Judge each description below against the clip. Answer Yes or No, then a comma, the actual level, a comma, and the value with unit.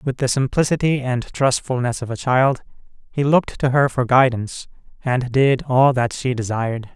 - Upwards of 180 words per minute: No, average, 175 wpm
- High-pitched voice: No, low, 130 Hz